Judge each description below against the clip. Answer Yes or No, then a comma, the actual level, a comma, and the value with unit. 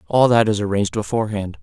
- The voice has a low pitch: Yes, low, 110 Hz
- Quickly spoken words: No, average, 185 wpm